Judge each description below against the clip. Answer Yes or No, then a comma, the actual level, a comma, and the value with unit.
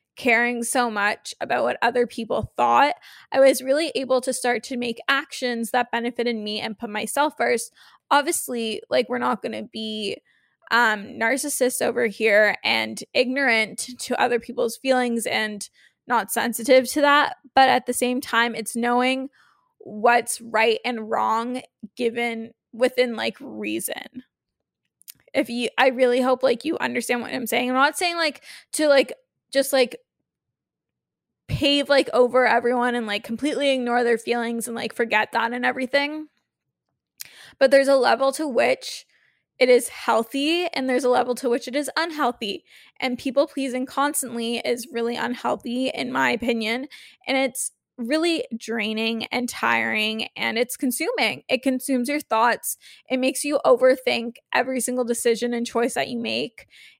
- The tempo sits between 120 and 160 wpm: Yes, average, 155 wpm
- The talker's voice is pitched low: No, high, 245 Hz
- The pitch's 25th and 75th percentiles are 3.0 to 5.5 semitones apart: No, narrow, 2.5 semitones